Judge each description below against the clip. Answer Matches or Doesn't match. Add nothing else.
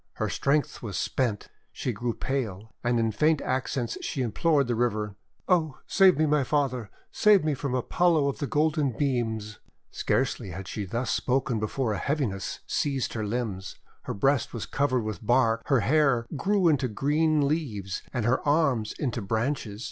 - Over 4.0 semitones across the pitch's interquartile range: Matches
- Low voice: Matches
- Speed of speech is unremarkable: Matches